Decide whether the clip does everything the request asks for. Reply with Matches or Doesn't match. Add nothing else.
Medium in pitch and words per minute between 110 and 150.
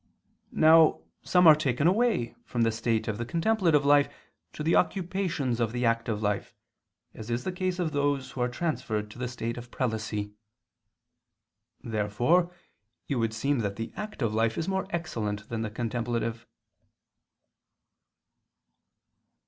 Doesn't match